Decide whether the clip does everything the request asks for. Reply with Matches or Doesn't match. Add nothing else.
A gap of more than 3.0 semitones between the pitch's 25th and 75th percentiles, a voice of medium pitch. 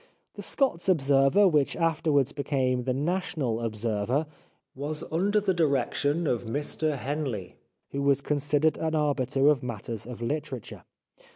Matches